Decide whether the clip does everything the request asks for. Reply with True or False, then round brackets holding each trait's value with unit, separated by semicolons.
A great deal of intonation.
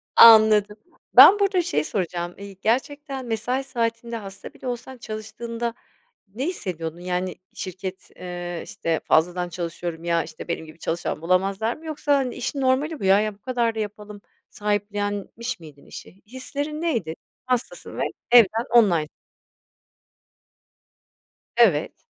True (5.8 semitones)